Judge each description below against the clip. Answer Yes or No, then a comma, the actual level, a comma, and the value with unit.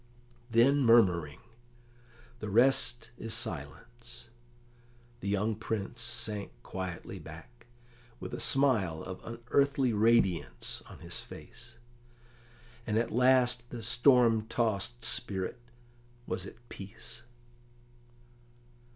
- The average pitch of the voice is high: No, low, 115 Hz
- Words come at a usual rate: No, slow, 100 wpm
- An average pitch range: Yes, average, 3.2 semitones